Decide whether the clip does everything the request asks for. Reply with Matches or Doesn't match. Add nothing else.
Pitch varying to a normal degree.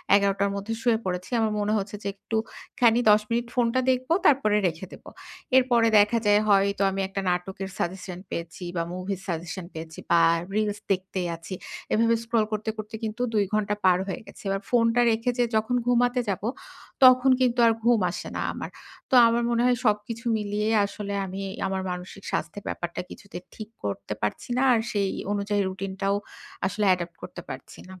Matches